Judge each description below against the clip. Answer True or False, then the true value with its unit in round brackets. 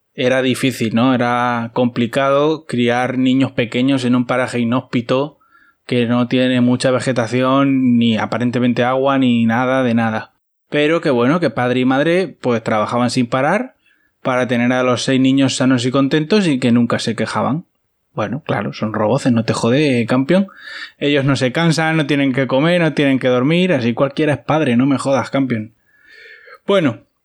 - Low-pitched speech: True (130 Hz)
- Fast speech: False (170 wpm)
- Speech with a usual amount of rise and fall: False (2.1 semitones)